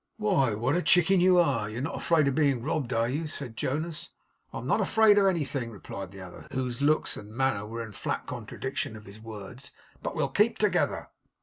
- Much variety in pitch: Yes, wide, 6.4 semitones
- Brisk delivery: Yes, fast, 215 wpm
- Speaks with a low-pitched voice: Yes, low, 130 Hz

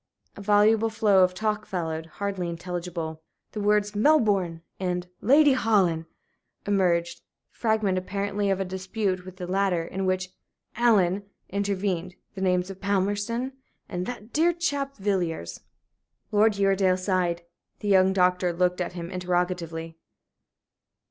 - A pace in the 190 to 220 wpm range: No, slow, 135 wpm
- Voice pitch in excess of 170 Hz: Yes, high, 190 Hz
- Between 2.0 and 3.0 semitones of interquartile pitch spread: Yes, narrow, 2.5 semitones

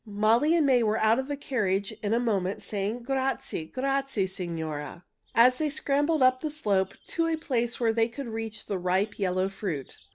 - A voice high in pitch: Yes, high, 225 Hz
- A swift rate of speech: No, average, 190 wpm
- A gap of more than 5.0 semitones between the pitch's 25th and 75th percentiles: Yes, wide, 5.5 semitones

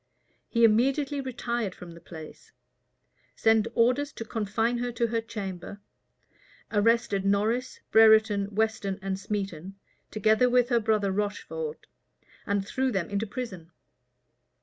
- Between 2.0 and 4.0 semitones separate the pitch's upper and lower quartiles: Yes, average, 3.1 semitones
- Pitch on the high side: Yes, high, 220 Hz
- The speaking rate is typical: No, slow, 125 wpm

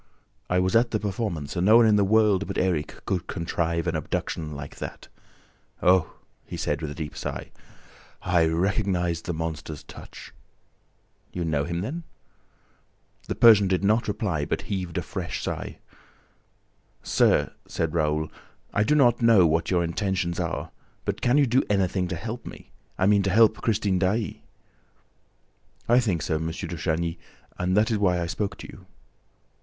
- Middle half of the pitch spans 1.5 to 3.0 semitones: No, average, 4.2 semitones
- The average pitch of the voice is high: No, very low, 90 Hz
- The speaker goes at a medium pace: Yes, average, 170 wpm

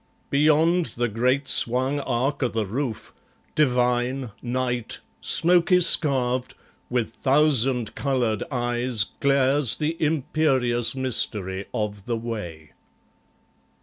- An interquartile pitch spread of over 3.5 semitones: No, average, 3.1 semitones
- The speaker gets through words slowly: Yes, slow, 100 wpm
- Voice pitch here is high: No, low, 125 Hz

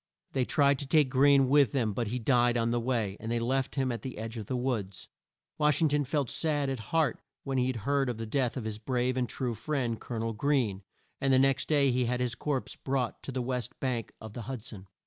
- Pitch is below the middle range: Yes, low, 125 Hz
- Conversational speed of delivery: No, fast, 250 wpm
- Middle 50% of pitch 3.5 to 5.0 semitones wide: No, average, 2.8 semitones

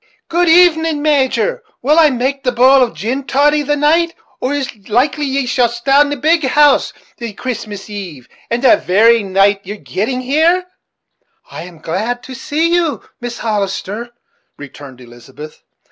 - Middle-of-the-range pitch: No, very high, 255 Hz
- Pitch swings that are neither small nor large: No, wide, 6.1 semitones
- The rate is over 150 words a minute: Yes, average, 160 wpm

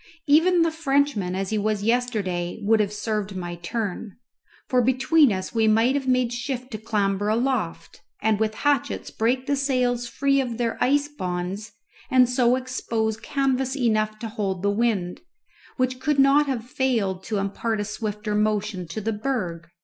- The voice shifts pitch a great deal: No, average, 3.9 semitones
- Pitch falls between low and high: No, high, 225 Hz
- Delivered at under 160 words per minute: No, average, 170 wpm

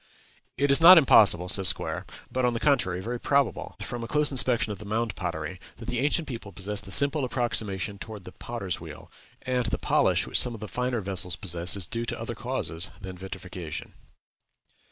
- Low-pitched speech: Yes, low, 110 Hz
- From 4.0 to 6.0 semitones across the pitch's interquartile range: Yes, average, 5.1 semitones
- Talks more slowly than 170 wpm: No, average, 195 wpm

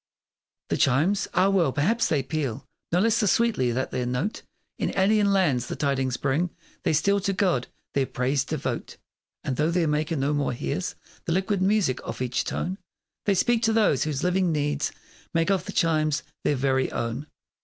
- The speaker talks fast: No, average, 185 wpm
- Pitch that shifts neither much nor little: No, wide, 6.2 semitones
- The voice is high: No, medium, 155 Hz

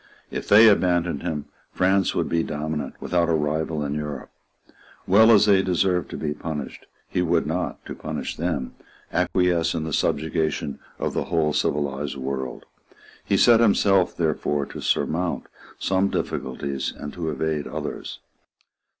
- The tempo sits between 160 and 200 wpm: No, average, 150 wpm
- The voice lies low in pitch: Yes, very low, 80 Hz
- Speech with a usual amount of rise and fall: Yes, average, 3.5 semitones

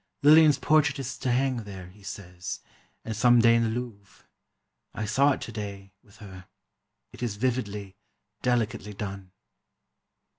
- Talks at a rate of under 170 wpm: Yes, average, 145 wpm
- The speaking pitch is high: No, low, 110 Hz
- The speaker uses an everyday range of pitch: Yes, average, 3.9 semitones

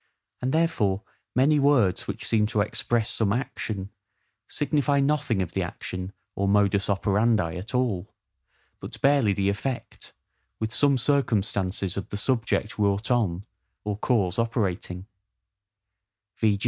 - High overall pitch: No, low, 105 Hz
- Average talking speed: No, slow, 130 wpm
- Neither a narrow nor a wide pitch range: Yes, average, 4.4 semitones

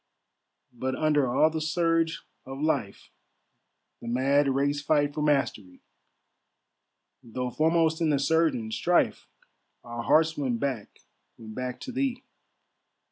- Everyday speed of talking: No, slow, 125 wpm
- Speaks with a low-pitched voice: No, medium, 145 Hz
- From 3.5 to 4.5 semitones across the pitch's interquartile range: Yes, average, 4.2 semitones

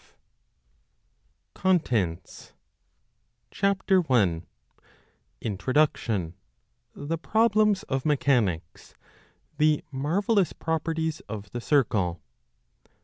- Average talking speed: No, slow, 85 wpm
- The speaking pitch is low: No, medium, 145 Hz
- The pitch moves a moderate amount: No, wide, 7.9 semitones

